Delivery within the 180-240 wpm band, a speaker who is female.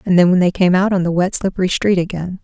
No: fast, 270 wpm; female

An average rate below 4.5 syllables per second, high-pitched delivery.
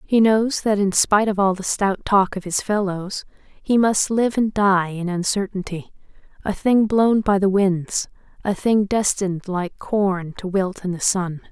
Yes: 4.2 syllables/s; high, 195 Hz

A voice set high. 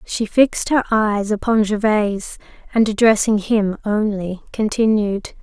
Yes: high, 210 Hz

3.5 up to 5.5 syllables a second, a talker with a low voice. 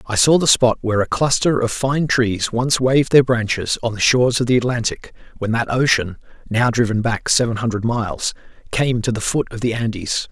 Yes: 4.6 syllables/s; low, 120 Hz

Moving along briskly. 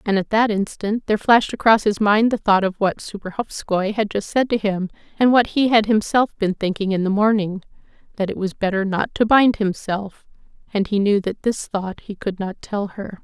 Yes: fast, 210 wpm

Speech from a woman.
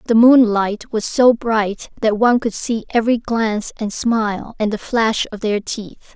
Yes: female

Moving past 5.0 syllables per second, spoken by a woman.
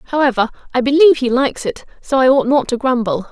Yes: 6.2 syllables/s; female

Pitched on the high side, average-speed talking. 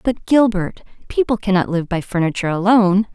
Yes: high, 200 Hz; average, 155 wpm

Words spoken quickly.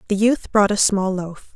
Yes: fast, 230 wpm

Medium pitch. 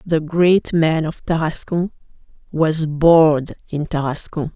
Yes: medium, 160 Hz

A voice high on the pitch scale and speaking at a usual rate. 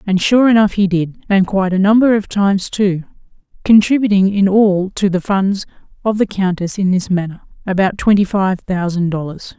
Yes: high, 195 Hz; average, 180 wpm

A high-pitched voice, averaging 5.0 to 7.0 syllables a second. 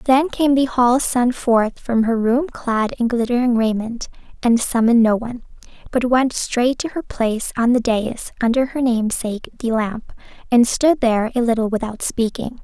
No: high, 240 Hz; 4.8 syllables/s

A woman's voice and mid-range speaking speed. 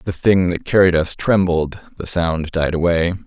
No: male; average, 165 wpm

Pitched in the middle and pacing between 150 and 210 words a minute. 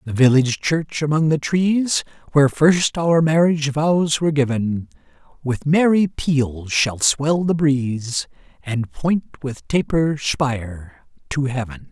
No: medium, 145 Hz; slow, 135 wpm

